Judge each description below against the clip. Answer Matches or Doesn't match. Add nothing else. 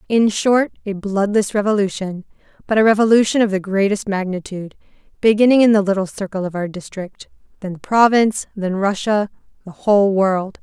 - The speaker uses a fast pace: Doesn't match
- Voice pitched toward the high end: Matches